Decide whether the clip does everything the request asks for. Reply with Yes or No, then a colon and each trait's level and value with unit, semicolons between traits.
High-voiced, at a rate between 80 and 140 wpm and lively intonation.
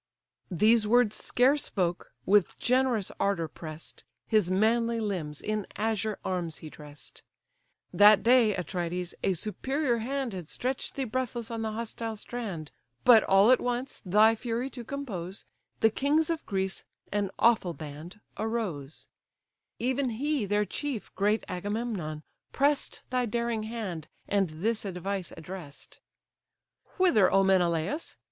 No: high, 215 Hz; slow, 135 wpm; average, 4.6 semitones